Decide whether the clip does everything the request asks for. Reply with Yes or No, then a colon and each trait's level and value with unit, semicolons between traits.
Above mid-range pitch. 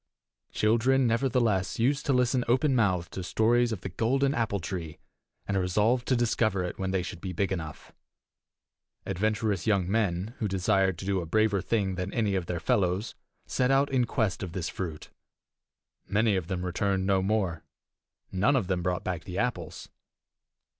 No: low, 100 Hz